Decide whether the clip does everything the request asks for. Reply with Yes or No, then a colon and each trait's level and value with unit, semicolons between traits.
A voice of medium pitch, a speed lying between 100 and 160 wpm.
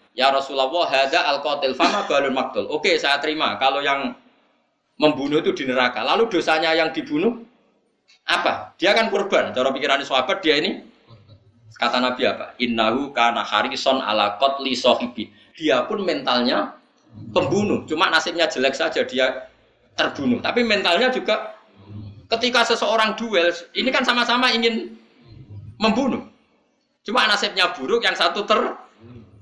Yes: medium, 160 Hz; average, 135 wpm